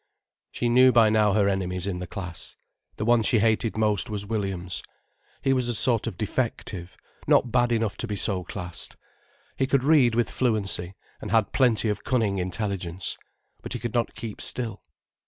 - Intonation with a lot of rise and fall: No, average, 3.5 semitones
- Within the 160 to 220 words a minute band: Yes, average, 180 wpm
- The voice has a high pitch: No, low, 110 Hz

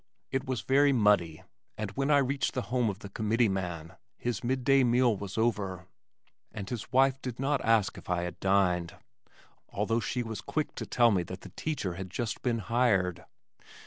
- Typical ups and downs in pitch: Yes, average, 4.8 semitones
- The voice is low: Yes, low, 115 Hz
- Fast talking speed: No, average, 185 wpm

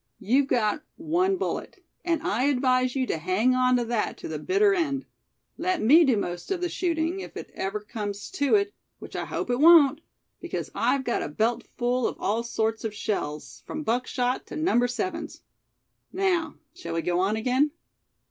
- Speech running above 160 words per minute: Yes, average, 185 wpm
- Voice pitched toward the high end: Yes, very high, 255 Hz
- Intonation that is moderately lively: No, wide, 6.8 semitones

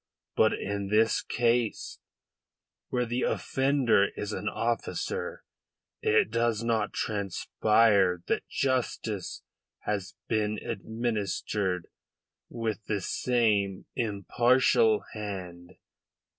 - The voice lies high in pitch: No, low, 110 Hz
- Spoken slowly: Yes, slow, 90 wpm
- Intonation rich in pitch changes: No, average, 2.8 semitones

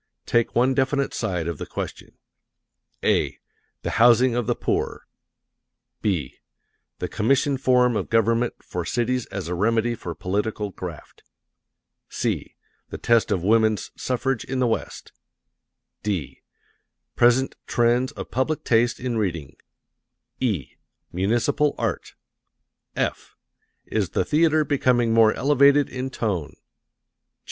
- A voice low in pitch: Yes, low, 115 Hz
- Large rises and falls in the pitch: No, average, 4.0 semitones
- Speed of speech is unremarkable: No, slow, 120 wpm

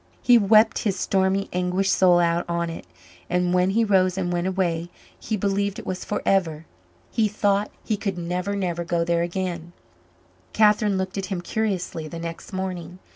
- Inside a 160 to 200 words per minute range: Yes, average, 175 wpm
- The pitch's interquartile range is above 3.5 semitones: No, narrow, 2.5 semitones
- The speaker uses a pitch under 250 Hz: Yes, medium, 185 Hz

